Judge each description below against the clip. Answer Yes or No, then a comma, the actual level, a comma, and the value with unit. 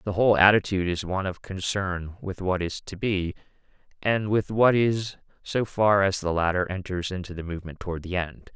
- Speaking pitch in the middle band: No, very low, 95 Hz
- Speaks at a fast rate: No, average, 195 wpm